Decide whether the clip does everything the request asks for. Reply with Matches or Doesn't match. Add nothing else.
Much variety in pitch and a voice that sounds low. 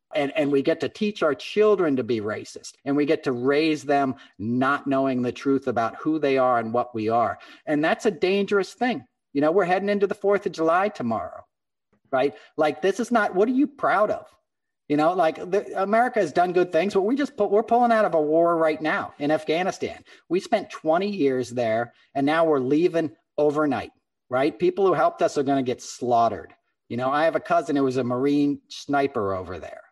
Doesn't match